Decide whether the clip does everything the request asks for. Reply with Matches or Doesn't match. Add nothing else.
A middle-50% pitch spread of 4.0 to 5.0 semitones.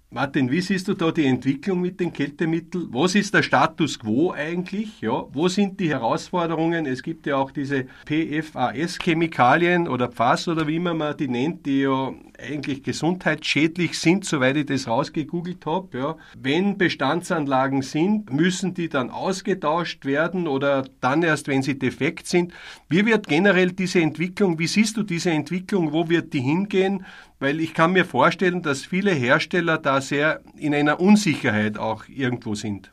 Matches